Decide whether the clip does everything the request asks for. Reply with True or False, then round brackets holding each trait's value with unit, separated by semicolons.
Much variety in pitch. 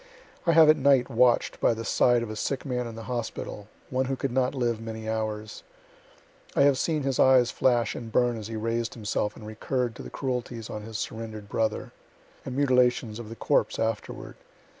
False (2.5 semitones)